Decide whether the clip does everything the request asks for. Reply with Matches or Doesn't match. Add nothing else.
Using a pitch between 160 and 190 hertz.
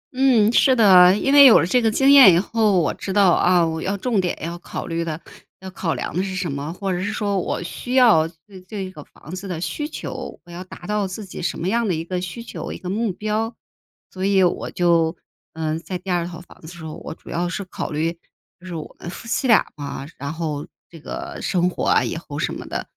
Matches